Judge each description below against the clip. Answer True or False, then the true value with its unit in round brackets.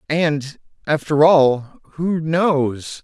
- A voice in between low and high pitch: True (150 Hz)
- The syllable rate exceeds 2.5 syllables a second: False (2.3 syllables/s)